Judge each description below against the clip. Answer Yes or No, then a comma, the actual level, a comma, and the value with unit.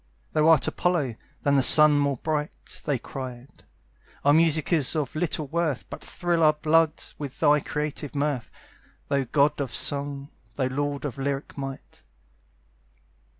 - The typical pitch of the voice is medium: Yes, medium, 145 Hz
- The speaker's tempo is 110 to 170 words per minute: Yes, average, 150 wpm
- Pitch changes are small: Yes, narrow, 1.9 semitones